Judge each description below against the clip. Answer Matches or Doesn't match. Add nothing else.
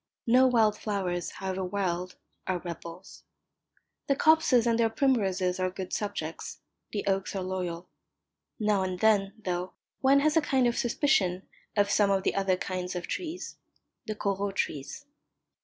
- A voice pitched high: Matches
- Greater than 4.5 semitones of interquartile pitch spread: Doesn't match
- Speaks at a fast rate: Doesn't match